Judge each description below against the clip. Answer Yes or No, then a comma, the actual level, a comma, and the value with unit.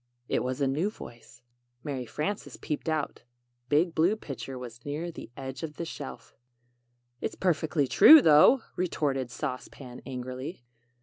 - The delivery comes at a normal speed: Yes, average, 160 wpm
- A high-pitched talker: No, medium, 145 Hz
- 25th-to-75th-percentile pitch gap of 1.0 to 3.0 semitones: No, average, 4.1 semitones